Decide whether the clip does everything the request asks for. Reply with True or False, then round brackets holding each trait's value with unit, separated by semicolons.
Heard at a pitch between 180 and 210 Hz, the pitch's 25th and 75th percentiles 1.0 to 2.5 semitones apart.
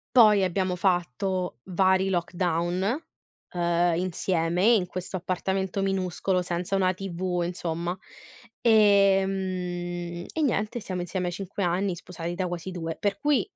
True (185 Hz; 1.8 semitones)